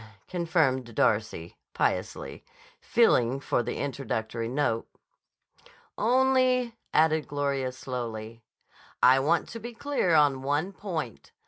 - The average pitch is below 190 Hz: Yes, medium, 140 Hz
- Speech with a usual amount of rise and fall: No, wide, 7.0 semitones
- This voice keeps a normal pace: No, slow, 105 wpm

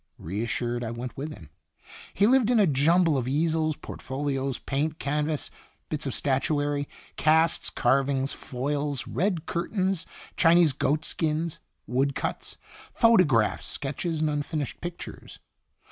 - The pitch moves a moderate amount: Yes, average, 3.4 semitones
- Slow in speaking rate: Yes, slow, 115 wpm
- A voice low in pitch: No, medium, 150 Hz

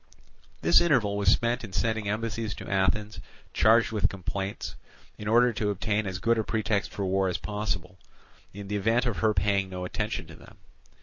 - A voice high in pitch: No, low, 105 Hz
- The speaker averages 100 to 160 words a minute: No, average, 185 wpm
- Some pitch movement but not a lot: No, narrow, 2.3 semitones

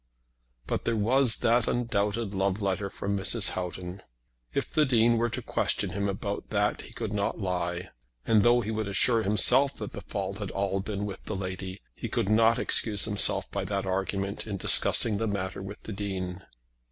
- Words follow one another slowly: No, average, 190 wpm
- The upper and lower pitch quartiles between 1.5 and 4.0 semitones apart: Yes, narrow, 2.4 semitones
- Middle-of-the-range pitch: No, low, 100 Hz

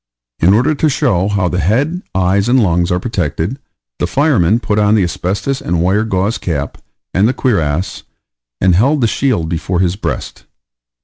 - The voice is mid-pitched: No, low, 100 Hz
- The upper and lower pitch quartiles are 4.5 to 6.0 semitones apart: Yes, average, 5.3 semitones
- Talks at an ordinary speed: Yes, average, 175 wpm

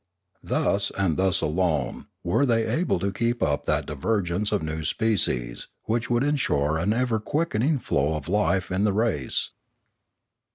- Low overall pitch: Yes, low, 100 Hz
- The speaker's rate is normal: Yes, average, 155 wpm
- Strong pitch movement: Yes, wide, 6.4 semitones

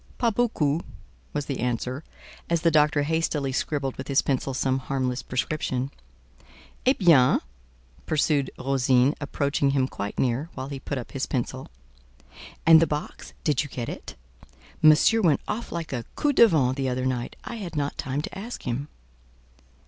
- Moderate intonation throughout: Yes, average, 3.3 semitones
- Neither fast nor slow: Yes, average, 165 wpm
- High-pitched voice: No, medium, 140 Hz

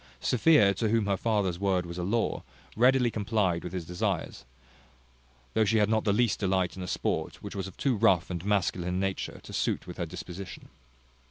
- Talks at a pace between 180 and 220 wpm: Yes, average, 200 wpm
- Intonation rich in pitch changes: No, average, 3.3 semitones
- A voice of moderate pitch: No, low, 100 Hz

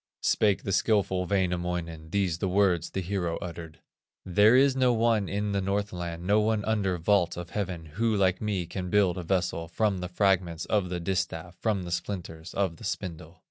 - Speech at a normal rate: Yes, average, 185 wpm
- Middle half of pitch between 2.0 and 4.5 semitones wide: Yes, average, 2.8 semitones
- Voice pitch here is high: No, very low, 95 Hz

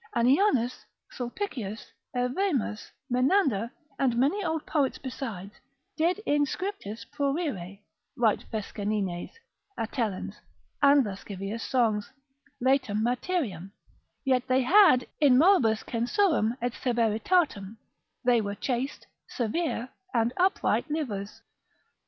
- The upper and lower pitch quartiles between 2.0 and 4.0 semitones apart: No, average, 5.1 semitones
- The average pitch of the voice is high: Yes, high, 245 Hz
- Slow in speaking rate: Yes, slow, 100 wpm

